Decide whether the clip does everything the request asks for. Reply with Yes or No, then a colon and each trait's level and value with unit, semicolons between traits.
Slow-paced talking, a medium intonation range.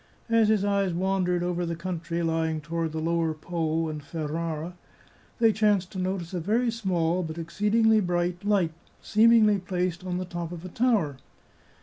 No: average, 170 wpm; average, 3.4 semitones